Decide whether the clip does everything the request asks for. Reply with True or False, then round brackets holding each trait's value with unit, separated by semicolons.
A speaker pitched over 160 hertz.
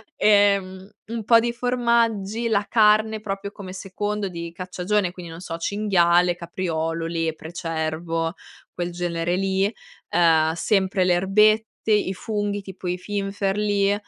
True (190 Hz)